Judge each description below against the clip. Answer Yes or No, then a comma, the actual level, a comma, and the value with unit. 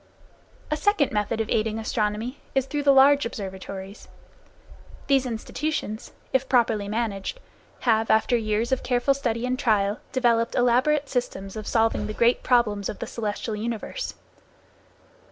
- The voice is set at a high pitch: Yes, high, 230 Hz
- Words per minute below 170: Yes, average, 140 wpm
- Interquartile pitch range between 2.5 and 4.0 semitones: Yes, average, 3.3 semitones